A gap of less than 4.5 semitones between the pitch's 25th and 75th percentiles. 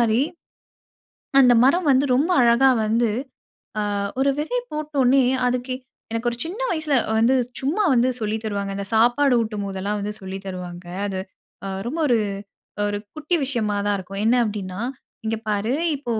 No: average, 4.8 semitones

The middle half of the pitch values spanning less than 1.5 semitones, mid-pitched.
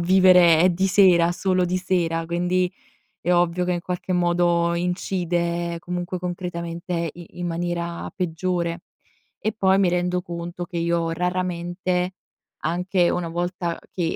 Yes: narrow, 1.0 semitones; medium, 175 Hz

